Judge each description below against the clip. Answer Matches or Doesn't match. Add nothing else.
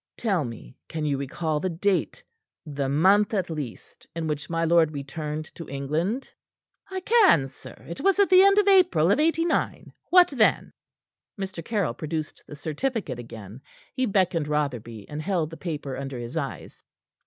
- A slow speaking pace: Doesn't match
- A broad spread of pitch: Matches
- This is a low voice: Doesn't match